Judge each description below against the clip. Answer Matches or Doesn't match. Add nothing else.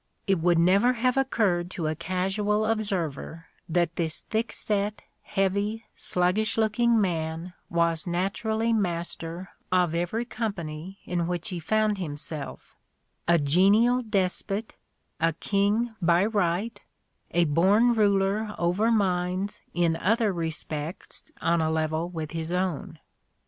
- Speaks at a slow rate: Matches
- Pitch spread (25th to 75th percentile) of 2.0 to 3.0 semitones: Doesn't match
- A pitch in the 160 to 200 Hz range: Matches